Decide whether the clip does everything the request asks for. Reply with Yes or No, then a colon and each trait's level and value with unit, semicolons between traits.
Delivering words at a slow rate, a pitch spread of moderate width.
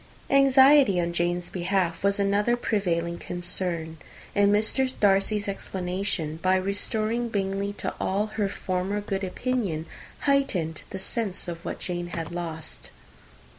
Yes: slow, 130 wpm; average, 3.1 semitones